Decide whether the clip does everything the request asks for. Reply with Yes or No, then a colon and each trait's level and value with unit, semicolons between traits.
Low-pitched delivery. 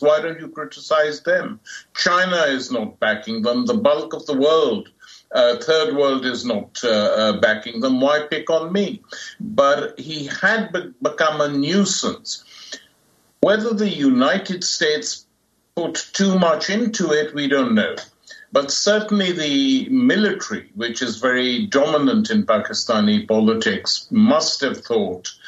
No: medium, 175 Hz